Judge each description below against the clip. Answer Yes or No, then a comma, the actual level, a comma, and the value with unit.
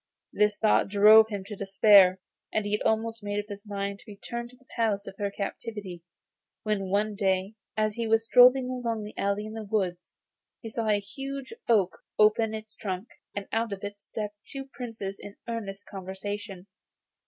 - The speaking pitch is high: Yes, high, 210 Hz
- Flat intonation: Yes, narrow, 2.0 semitones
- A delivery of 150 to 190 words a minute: Yes, average, 185 wpm